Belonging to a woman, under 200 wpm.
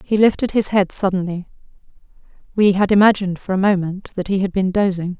Yes: female; average, 185 wpm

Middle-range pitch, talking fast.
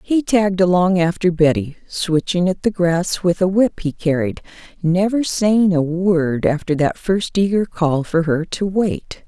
No: medium, 180 Hz; average, 175 wpm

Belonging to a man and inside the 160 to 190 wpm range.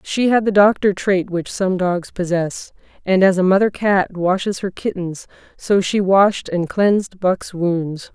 No: female; average, 175 wpm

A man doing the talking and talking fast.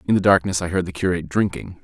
Yes: male; fast, 260 wpm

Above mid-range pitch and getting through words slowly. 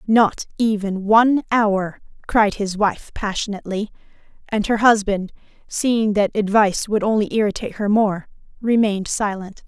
Yes: high, 210 Hz; slow, 130 wpm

